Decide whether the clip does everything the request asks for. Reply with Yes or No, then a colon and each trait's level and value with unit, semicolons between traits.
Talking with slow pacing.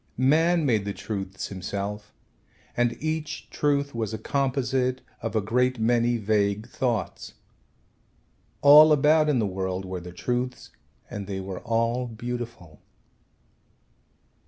Yes: slow, 125 wpm